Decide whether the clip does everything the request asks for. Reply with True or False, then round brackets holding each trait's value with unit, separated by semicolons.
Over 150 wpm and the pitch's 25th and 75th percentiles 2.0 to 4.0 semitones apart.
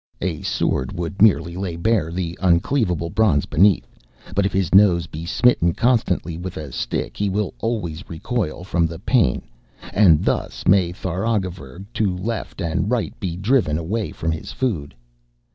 True (160 wpm; 3.7 semitones)